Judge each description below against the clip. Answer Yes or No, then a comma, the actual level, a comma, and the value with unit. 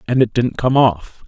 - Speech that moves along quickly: Yes, fast, 235 wpm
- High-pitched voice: No, low, 120 Hz